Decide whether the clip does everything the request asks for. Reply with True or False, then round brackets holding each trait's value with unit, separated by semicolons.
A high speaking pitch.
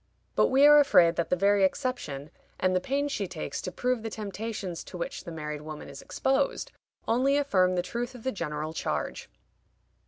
True (195 Hz)